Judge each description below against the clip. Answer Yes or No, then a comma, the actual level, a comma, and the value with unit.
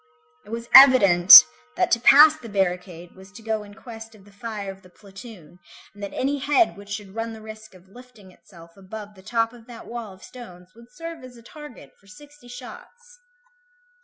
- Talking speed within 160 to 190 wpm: No, average, 200 wpm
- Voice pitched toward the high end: Yes, high, 220 Hz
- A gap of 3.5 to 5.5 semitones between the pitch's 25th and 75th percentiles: Yes, average, 4.1 semitones